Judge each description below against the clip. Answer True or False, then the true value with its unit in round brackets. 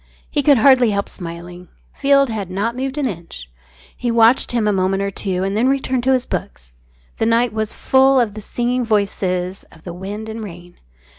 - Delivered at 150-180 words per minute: False (200 wpm)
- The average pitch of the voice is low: False (220 Hz)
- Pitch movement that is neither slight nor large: True (5.0 semitones)